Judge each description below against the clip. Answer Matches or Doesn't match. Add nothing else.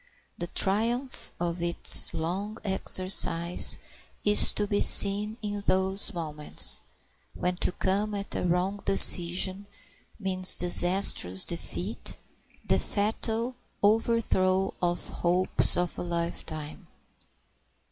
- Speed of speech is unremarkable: Doesn't match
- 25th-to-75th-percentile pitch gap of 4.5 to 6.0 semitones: Doesn't match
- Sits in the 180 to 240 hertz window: Matches